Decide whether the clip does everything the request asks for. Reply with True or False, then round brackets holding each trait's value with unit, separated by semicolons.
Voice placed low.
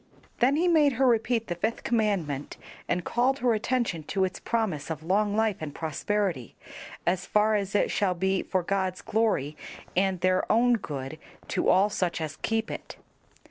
False (195 Hz)